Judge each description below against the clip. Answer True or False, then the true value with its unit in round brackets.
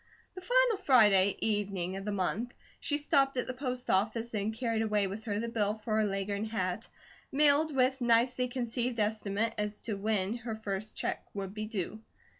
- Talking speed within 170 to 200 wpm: True (185 wpm)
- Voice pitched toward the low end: False (220 Hz)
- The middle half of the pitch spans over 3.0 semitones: True (3.5 semitones)